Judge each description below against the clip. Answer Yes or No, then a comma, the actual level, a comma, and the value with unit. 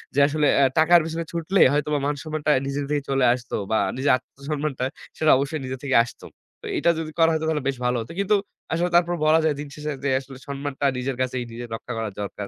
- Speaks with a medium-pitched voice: Yes, medium, 145 Hz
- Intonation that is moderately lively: Yes, average, 3.2 semitones